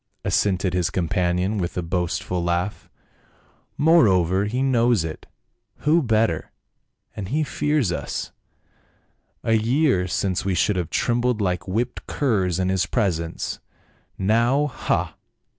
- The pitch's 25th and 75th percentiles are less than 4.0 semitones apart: No, average, 5.0 semitones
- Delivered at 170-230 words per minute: No, slow, 135 wpm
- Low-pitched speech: Yes, low, 100 Hz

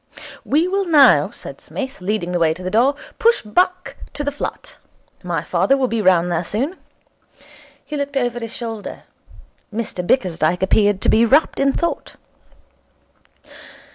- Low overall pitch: No, high, 235 Hz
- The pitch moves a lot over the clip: Yes, wide, 7.2 semitones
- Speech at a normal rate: Yes, average, 155 wpm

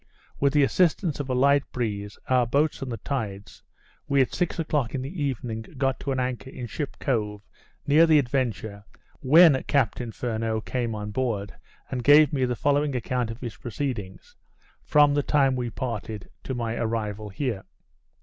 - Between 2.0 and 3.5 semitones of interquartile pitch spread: No, average, 4.0 semitones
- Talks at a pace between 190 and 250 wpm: No, average, 175 wpm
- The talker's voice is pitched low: Yes, low, 125 Hz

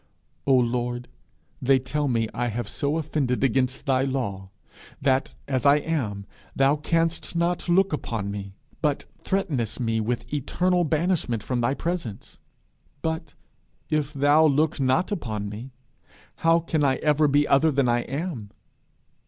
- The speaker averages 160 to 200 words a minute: No, average, 145 wpm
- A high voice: No, low, 135 Hz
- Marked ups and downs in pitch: No, average, 4.4 semitones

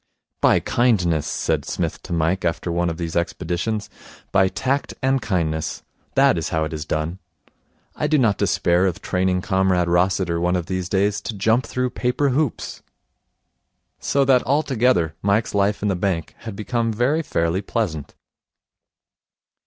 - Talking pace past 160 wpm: No, average, 155 wpm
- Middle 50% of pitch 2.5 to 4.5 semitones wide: No, average, 5.2 semitones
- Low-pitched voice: Yes, very low, 95 Hz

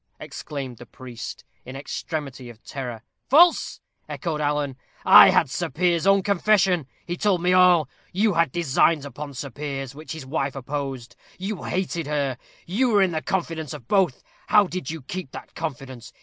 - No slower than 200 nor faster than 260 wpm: No, average, 170 wpm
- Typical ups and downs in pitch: Yes, average, 5.0 semitones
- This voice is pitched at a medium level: Yes, medium, 155 Hz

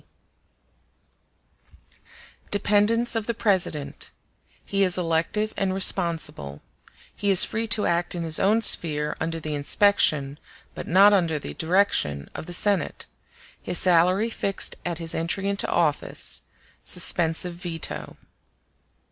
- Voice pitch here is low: No, medium, 175 Hz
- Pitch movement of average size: Yes, average, 3.8 semitones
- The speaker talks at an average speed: No, slow, 115 wpm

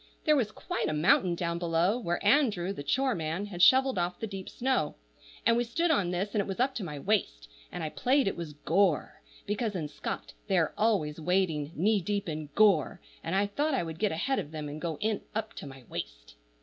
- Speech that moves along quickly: Yes, fast, 225 wpm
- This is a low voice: No, high, 190 Hz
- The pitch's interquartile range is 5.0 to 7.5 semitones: Yes, average, 5.3 semitones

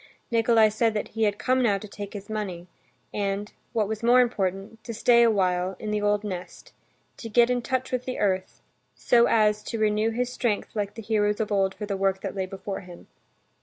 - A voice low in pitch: No, high, 210 Hz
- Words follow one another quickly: Yes, fast, 215 wpm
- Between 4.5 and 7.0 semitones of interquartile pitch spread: No, narrow, 2.6 semitones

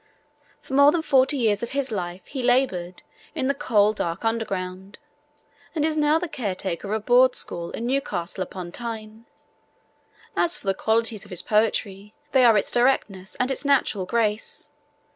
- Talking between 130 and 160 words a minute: No, average, 170 wpm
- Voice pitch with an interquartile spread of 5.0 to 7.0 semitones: Yes, average, 5.3 semitones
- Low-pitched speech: No, high, 225 Hz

